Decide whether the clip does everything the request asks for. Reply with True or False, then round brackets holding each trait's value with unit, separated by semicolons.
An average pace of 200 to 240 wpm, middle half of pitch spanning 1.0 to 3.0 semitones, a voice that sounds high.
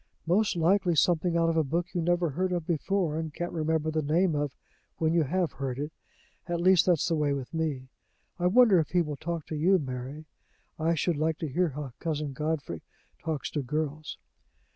False (205 wpm; 2.7 semitones; 160 Hz)